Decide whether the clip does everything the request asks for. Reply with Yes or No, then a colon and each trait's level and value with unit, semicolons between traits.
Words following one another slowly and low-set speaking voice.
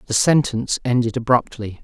Yes: slow, 130 wpm; low, 120 Hz